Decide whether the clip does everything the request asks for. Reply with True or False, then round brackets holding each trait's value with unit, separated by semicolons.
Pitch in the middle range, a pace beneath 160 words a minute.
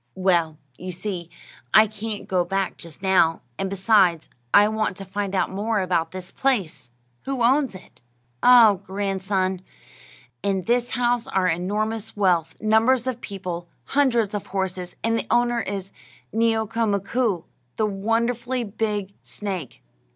False (200 Hz; 140 wpm)